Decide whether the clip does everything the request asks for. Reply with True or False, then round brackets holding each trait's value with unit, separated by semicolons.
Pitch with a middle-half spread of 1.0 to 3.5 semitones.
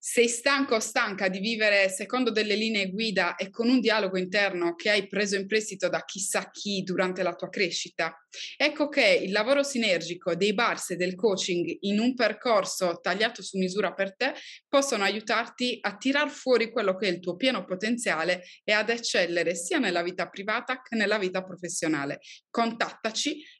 False (4.0 semitones)